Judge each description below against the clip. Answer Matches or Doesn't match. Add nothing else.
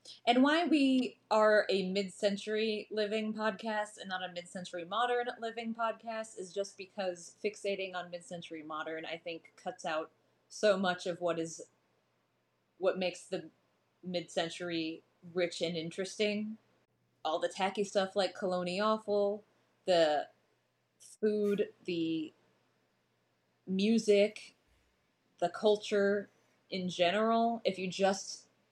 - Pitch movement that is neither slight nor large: Matches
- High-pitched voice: Matches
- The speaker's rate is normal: Doesn't match